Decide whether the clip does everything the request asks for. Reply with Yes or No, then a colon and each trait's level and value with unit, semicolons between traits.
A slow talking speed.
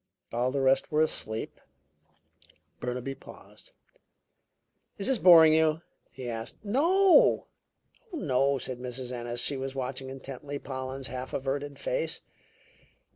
Yes: slow, 120 wpm